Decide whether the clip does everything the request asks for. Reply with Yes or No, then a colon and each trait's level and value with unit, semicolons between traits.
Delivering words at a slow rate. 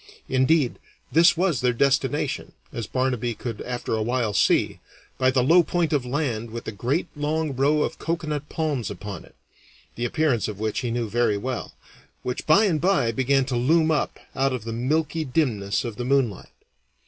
No: average, 185 wpm